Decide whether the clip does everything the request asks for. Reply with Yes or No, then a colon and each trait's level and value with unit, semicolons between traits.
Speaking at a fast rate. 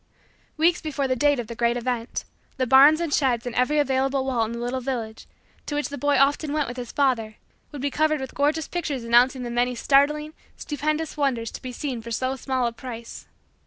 Yes: fast, 215 wpm